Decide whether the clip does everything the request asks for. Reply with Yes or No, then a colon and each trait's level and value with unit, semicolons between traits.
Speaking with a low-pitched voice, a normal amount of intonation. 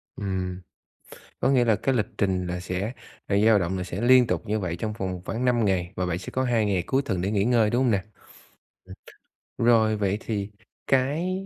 Yes: low, 105 Hz; average, 4.6 semitones